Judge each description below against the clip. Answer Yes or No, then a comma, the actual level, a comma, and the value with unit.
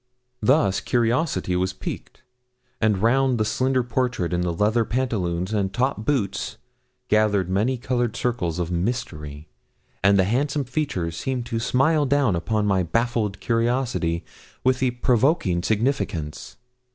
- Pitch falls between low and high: No, low, 115 Hz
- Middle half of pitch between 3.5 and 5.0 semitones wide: No, wide, 5.4 semitones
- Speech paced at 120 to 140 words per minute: Yes, slow, 135 wpm